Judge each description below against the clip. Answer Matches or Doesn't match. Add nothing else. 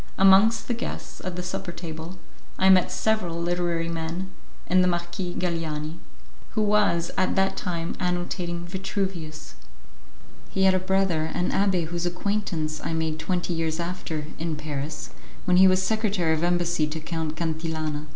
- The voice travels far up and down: Doesn't match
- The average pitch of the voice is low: Doesn't match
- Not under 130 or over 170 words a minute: Matches